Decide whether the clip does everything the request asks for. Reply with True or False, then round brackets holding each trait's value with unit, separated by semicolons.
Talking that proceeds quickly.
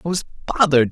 False (195 wpm)